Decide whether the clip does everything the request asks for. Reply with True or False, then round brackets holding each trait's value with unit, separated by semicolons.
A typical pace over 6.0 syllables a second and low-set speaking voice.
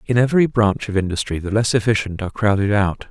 True (6.4 syllables/s; 105 Hz)